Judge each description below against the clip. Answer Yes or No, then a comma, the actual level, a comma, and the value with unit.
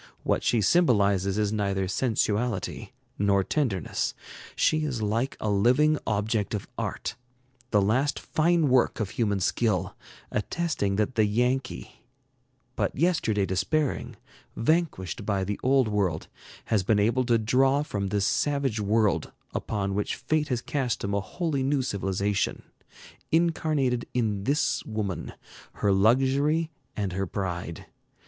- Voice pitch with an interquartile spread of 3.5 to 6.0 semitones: Yes, average, 5.2 semitones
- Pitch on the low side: Yes, low, 110 Hz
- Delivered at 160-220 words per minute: No, slow, 135 wpm